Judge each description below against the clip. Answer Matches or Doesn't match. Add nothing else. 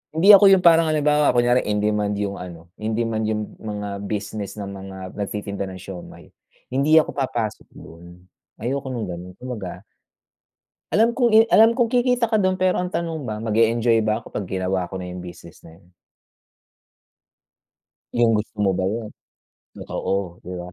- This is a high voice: Doesn't match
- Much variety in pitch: Matches